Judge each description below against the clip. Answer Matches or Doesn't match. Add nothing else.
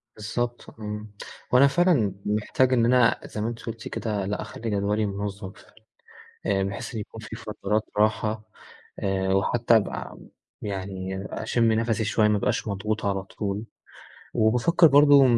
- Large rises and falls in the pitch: Doesn't match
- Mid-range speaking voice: Doesn't match